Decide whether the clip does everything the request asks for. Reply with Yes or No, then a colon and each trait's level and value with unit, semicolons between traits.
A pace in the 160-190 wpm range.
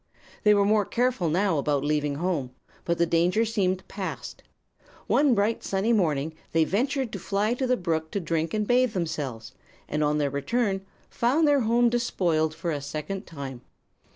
Yes: average, 175 wpm